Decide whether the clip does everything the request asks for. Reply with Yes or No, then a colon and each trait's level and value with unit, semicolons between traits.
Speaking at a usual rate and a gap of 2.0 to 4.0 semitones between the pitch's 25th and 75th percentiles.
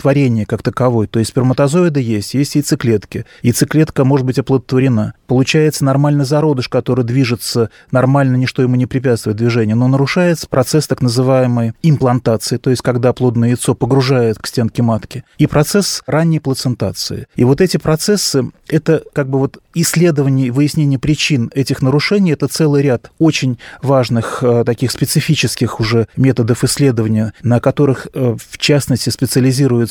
Yes: average, 145 wpm; average, 3.1 semitones